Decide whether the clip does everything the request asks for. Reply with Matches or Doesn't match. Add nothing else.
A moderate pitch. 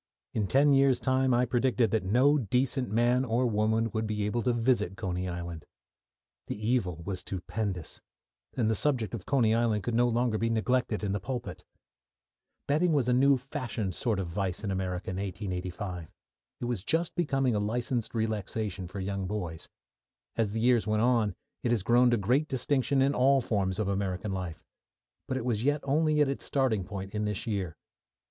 Doesn't match